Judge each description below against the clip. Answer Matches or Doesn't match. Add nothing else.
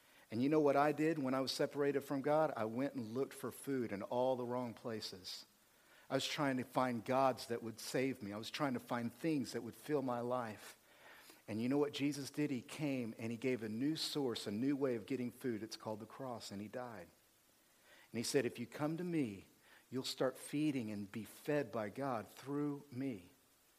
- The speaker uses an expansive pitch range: Doesn't match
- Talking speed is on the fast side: Matches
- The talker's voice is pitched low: Matches